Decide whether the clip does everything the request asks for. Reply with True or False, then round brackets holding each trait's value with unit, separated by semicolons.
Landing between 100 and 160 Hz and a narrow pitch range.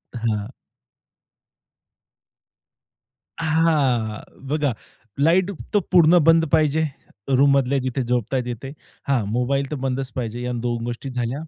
False (135 Hz; 3.9 semitones)